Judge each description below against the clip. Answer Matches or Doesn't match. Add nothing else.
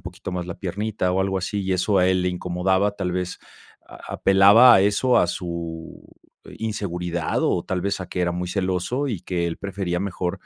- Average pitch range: Doesn't match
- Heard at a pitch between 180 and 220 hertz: Doesn't match